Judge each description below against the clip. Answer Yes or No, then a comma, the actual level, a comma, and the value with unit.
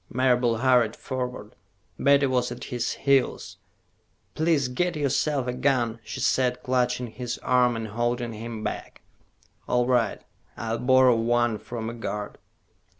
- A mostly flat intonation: Yes, narrow, 1.8 semitones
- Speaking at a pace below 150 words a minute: Yes, average, 140 wpm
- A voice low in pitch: Yes, low, 125 Hz